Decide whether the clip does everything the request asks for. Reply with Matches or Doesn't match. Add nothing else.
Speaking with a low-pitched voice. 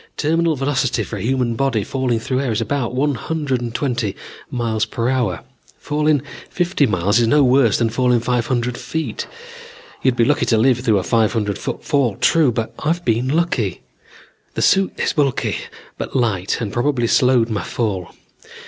Matches